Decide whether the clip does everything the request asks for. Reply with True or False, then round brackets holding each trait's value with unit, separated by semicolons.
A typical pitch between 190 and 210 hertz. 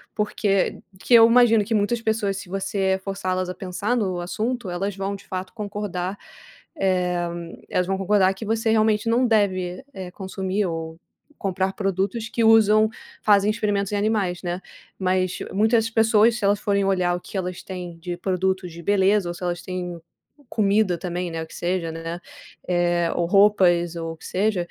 True (195 Hz)